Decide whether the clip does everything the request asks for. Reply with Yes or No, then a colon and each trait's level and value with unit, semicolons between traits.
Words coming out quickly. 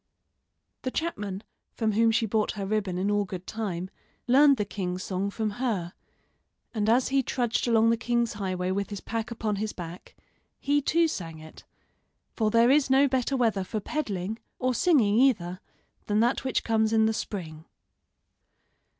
No: average, 170 wpm